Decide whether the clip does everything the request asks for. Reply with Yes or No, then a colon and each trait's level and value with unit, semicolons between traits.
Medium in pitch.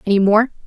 No: high, 210 Hz